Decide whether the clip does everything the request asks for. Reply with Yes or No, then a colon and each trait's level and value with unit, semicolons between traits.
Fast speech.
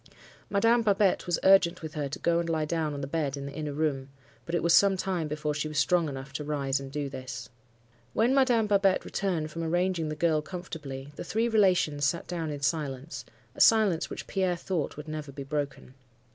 Yes: fast, 215 wpm